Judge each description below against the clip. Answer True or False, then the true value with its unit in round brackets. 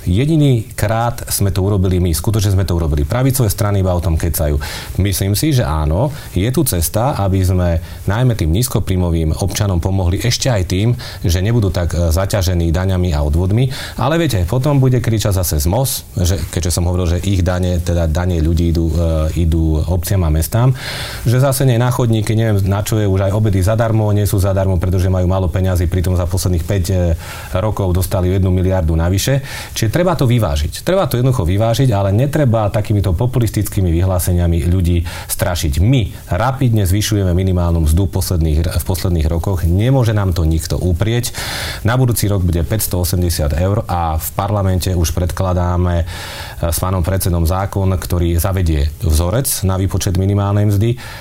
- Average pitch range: True (4.0 semitones)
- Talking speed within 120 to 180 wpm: True (165 wpm)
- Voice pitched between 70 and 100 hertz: True (95 Hz)